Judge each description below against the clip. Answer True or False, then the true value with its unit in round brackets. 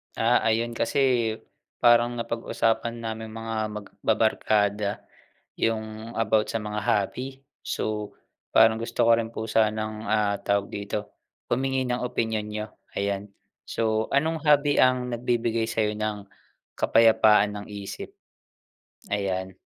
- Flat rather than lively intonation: True (1.8 semitones)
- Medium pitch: False (110 Hz)